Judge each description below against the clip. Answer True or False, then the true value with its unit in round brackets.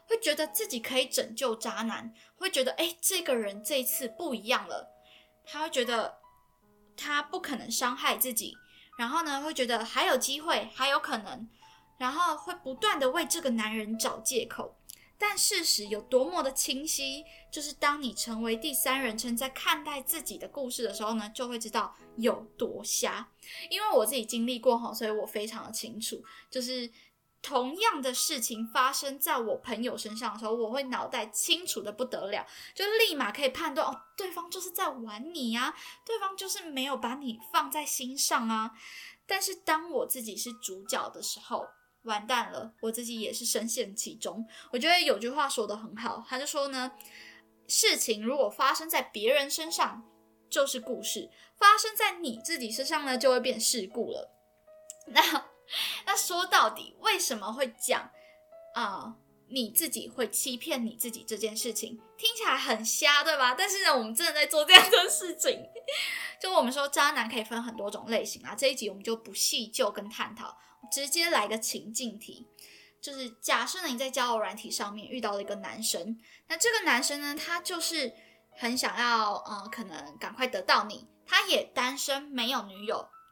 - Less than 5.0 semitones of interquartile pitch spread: False (5.5 semitones)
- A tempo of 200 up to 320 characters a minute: True (270 characters per minute)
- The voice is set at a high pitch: True (255 Hz)